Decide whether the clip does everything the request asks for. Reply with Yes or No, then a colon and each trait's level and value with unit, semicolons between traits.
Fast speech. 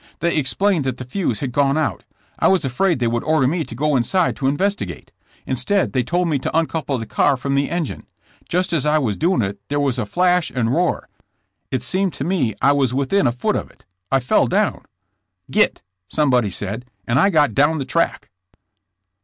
Yes: fast, 210 wpm